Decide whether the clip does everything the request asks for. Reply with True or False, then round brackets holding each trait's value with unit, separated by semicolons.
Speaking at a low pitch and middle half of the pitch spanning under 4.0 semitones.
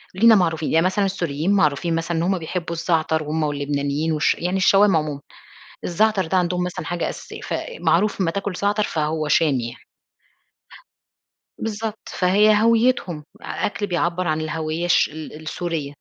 False (170 Hz; 3.6 semitones)